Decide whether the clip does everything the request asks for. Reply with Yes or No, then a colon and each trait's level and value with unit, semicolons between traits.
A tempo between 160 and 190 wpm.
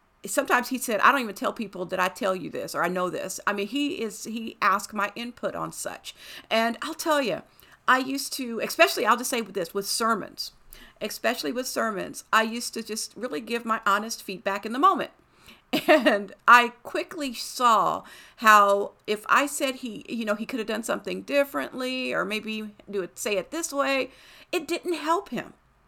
No: average, 200 wpm